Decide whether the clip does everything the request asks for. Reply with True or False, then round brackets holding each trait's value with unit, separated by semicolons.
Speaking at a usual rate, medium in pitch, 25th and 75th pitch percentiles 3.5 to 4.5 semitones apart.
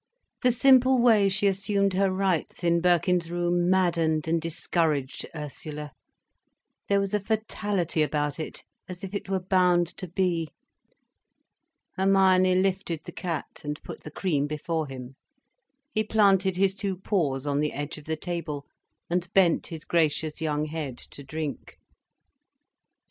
True (145 wpm; 175 Hz; 3.8 semitones)